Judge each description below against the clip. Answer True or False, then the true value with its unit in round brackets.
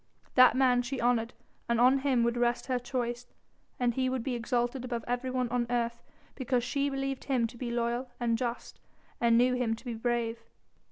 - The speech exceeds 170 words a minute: True (190 wpm)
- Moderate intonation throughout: False (1.3 semitones)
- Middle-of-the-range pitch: False (245 Hz)